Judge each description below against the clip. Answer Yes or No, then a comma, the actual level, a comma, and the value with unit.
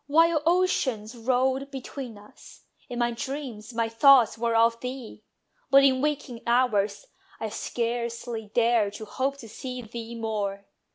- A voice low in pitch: No, high, 235 Hz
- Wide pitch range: No, average, 2.8 semitones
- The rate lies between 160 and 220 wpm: No, average, 145 wpm